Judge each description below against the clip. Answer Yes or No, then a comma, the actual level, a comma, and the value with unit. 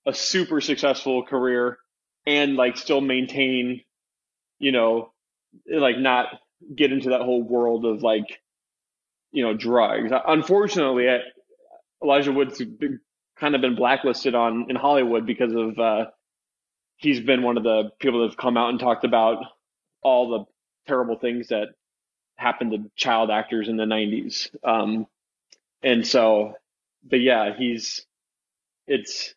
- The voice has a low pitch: Yes, low, 125 Hz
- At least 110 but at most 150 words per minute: Yes, average, 140 wpm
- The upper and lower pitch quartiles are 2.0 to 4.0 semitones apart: Yes, average, 3.1 semitones